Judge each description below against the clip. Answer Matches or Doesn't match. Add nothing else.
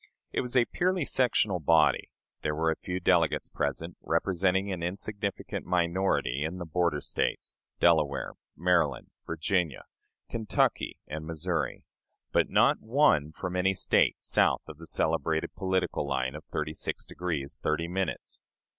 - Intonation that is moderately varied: Matches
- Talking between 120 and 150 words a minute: Matches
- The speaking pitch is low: Matches